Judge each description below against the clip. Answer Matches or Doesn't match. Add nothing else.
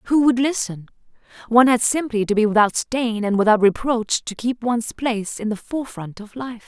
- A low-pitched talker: Doesn't match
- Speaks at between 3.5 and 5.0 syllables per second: Doesn't match